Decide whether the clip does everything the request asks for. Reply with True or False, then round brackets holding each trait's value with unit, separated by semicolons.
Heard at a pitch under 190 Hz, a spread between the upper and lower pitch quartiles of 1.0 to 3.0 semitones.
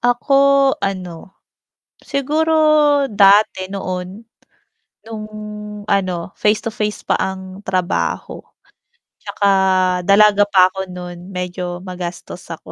False (195 Hz; 2.7 semitones)